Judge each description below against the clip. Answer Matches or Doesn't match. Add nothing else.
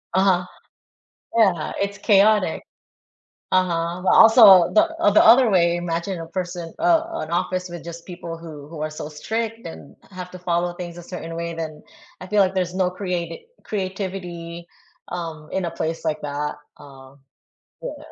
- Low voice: Doesn't match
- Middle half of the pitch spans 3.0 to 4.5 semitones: Doesn't match